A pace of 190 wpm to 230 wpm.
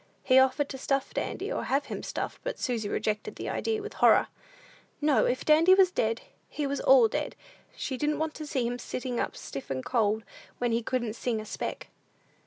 Yes: average, 200 wpm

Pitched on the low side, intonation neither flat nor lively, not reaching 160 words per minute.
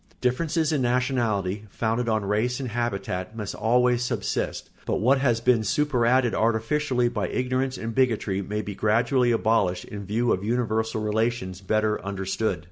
Yes: low, 115 Hz; average, 3.0 semitones; average, 150 wpm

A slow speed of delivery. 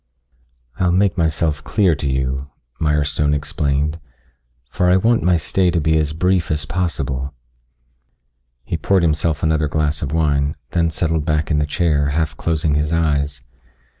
No: average, 155 wpm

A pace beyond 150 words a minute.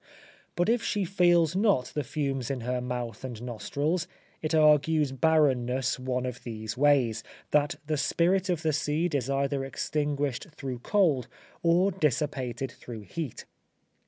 No: average, 145 wpm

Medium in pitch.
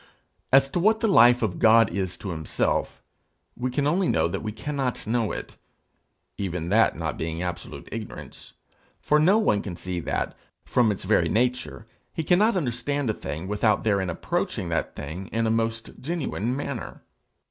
No: low, 115 Hz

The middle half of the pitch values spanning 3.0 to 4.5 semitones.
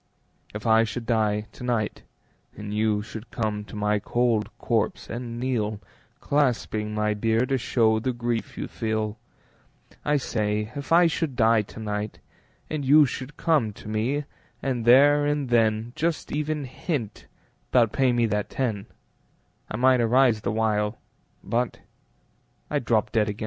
Yes: average, 3.4 semitones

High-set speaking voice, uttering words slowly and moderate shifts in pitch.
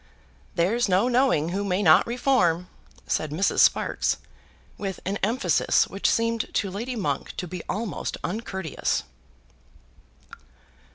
Yes: high, 200 Hz; slow, 120 wpm; average, 4.2 semitones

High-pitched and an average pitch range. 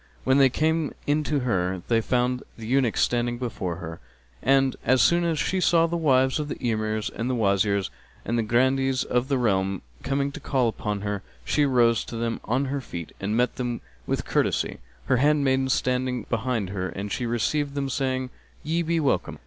No: low, 125 Hz; average, 3.7 semitones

